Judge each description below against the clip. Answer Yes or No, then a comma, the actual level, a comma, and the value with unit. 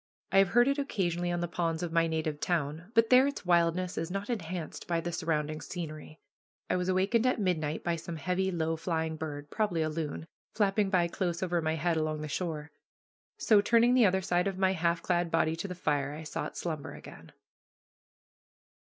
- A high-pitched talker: No, medium, 175 Hz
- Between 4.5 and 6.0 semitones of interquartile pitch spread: No, average, 3.0 semitones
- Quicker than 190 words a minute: Yes, average, 200 wpm